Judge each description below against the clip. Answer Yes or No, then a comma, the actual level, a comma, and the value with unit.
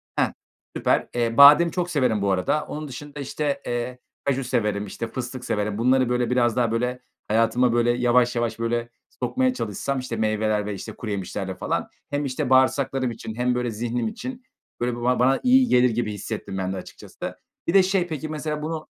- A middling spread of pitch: Yes, average, 3.7 semitones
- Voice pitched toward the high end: No, low, 125 Hz